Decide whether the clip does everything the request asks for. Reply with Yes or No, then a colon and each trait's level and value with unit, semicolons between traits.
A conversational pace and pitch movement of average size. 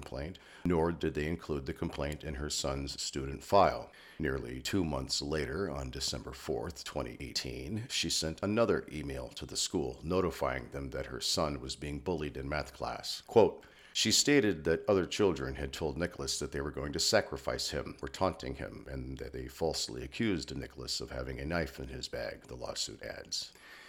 Yes: average, 185 wpm; average, 3.6 semitones